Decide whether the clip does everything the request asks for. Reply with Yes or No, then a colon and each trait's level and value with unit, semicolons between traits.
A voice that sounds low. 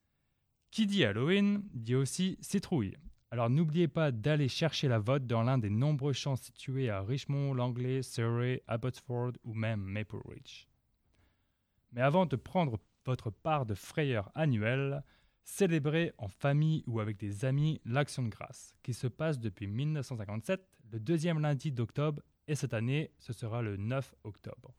Yes: low, 130 Hz